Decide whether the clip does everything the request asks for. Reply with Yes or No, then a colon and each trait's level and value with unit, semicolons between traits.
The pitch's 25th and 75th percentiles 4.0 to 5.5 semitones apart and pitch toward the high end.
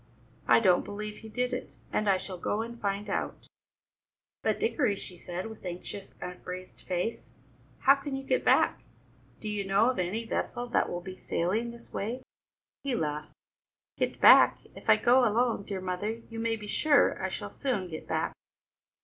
Yes: average, 4.3 semitones; high, 210 Hz